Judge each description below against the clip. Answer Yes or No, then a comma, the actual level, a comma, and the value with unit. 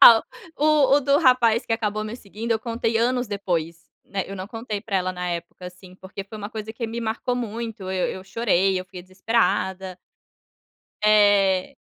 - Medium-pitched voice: No, high, 210 Hz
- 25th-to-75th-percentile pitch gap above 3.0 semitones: Yes, average, 3.6 semitones